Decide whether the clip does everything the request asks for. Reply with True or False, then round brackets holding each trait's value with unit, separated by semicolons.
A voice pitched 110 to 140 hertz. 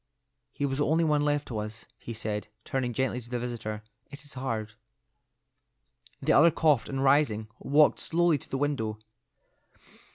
True (135 Hz)